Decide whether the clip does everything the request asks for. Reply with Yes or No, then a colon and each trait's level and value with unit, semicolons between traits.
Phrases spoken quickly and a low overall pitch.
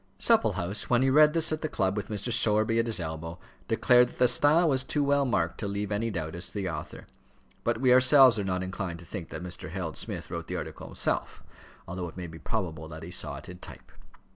Yes: fast, 240 wpm; low, 100 Hz